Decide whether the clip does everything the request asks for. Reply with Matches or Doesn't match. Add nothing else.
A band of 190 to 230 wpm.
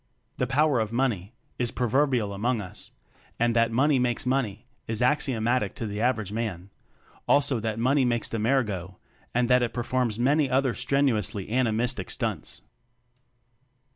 Doesn't match